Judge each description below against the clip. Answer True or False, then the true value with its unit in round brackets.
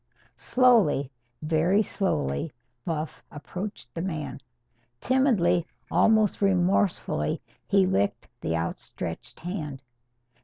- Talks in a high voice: False (165 Hz)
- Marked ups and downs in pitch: True (7.7 semitones)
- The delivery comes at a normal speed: False (85 wpm)